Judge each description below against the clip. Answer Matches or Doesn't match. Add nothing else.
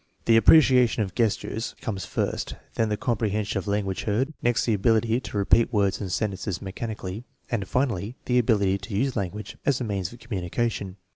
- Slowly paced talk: Doesn't match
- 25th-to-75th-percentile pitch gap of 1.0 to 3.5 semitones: Matches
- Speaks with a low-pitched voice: Matches